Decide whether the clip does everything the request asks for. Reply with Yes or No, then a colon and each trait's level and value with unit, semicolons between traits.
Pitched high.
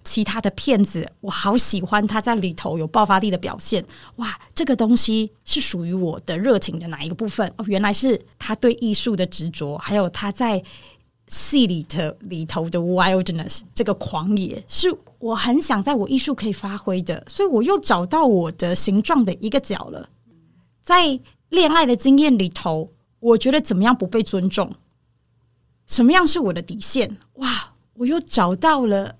Yes: high, 210 Hz